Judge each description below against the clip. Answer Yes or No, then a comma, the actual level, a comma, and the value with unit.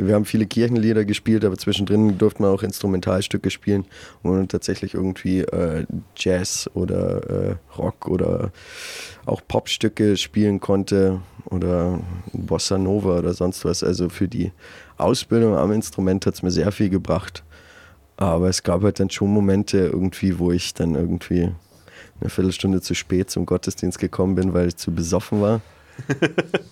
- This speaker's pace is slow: No, average, 155 wpm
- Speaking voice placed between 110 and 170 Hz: No, very low, 95 Hz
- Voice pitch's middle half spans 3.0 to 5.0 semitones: No, narrow, 2.6 semitones